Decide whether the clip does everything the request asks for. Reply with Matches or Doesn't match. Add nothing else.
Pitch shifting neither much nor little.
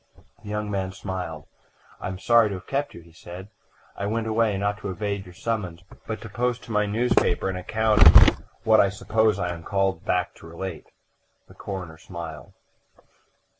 Matches